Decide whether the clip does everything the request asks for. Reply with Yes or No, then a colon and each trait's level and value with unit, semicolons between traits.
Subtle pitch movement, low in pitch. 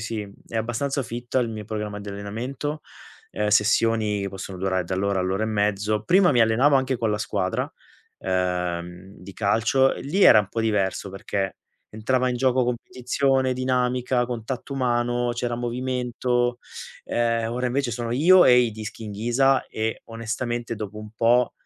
No: average, 3.1 semitones; low, 115 Hz